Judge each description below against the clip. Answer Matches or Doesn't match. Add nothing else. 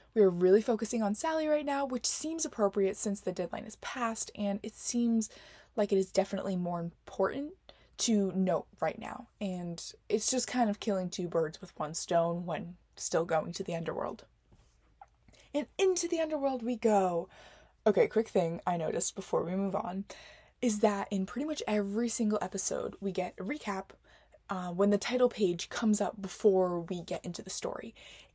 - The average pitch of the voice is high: Matches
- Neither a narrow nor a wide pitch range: Matches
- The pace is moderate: Matches